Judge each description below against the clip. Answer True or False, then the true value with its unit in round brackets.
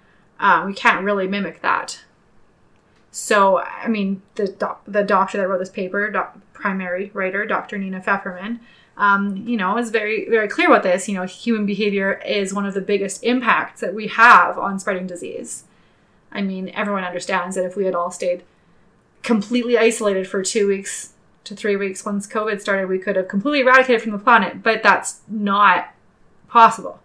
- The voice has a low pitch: False (200 Hz)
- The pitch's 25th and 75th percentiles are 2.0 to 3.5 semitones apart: True (2.4 semitones)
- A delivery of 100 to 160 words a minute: False (180 wpm)